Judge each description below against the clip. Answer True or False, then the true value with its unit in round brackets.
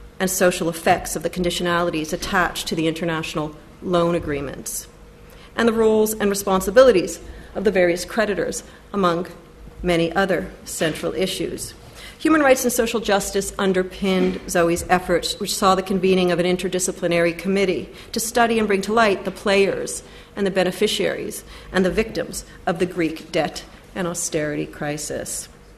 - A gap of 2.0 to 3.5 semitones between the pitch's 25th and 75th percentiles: True (2.5 semitones)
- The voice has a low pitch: False (185 Hz)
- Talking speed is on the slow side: False (145 wpm)